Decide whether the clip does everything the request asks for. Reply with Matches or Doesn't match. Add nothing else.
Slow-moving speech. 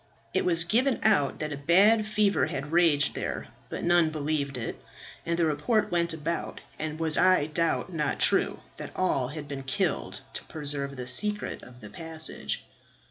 Doesn't match